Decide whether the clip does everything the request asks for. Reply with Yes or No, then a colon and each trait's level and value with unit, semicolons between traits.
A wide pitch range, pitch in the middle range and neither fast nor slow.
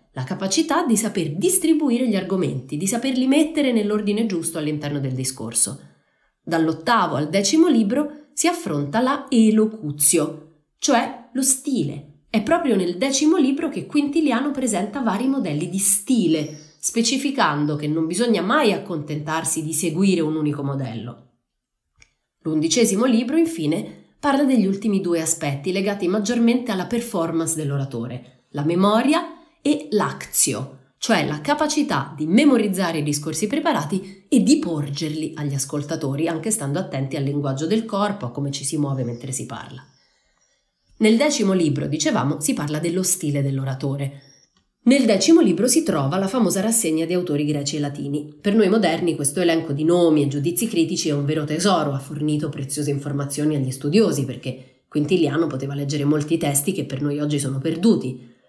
Yes: wide, 7.6 semitones; medium, 165 Hz; average, 150 wpm